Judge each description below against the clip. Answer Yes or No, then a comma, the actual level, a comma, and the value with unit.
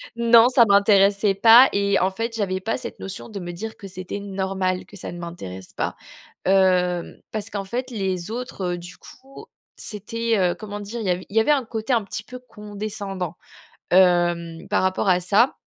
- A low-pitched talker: No, high, 200 Hz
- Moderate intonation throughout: Yes, average, 3.4 semitones